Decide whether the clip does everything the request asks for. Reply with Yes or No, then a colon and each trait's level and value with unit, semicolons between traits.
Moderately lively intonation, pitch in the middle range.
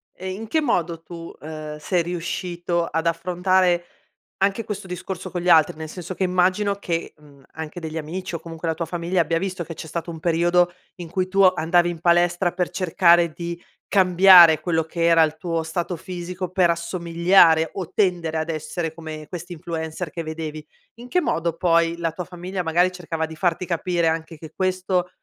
No: narrow, 1.9 semitones; medium, 170 Hz